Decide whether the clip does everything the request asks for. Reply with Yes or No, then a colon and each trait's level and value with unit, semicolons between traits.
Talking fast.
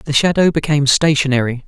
No: average, 145 wpm